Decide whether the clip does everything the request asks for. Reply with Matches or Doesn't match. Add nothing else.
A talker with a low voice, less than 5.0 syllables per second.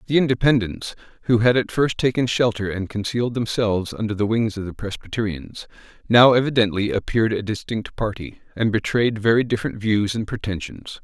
Doesn't match